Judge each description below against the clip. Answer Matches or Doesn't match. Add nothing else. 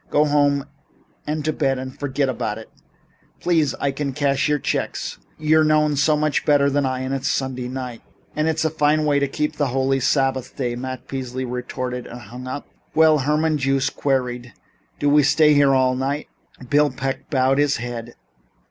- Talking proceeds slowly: Doesn't match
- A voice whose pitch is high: Doesn't match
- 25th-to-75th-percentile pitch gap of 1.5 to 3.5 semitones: Matches